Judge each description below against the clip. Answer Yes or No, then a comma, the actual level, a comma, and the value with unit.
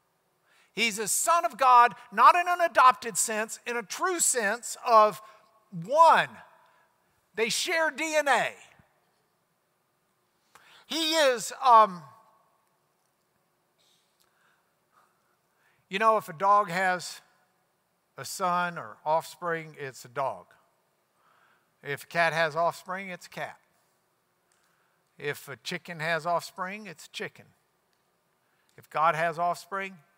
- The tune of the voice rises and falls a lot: Yes, wide, 5.9 semitones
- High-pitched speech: Yes, high, 195 Hz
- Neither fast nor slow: No, slow, 110 wpm